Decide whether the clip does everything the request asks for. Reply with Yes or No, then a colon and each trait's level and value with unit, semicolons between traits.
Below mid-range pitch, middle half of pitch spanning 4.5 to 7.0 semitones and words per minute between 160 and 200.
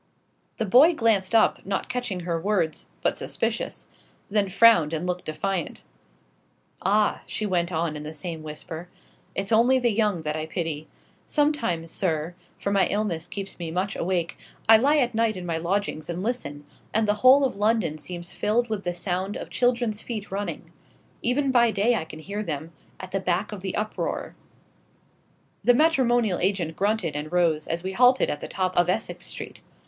No: high, 195 Hz; average, 4.8 semitones; average, 185 wpm